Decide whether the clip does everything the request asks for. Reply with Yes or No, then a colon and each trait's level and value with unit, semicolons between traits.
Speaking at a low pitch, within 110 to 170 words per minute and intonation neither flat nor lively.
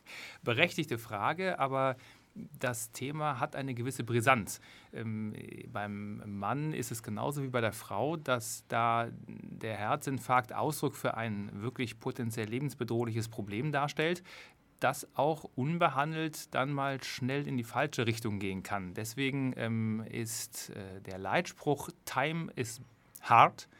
Yes: low, 125 Hz; average, 130 wpm; average, 3.8 semitones